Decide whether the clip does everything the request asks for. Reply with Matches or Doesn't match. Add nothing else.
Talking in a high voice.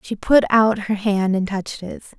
Matches